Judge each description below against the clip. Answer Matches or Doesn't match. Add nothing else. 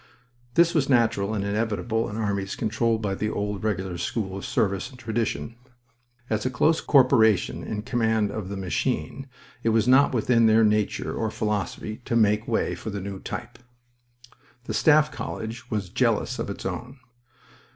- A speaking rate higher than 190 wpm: Doesn't match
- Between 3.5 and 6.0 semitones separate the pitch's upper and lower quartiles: Doesn't match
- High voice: Doesn't match